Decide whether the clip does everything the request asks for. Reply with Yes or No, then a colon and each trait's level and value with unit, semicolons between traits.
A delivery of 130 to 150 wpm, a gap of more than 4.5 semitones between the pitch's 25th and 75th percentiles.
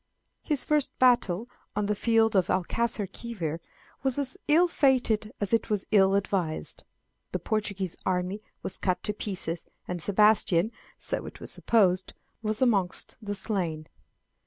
No: average, 140 wpm; average, 3.7 semitones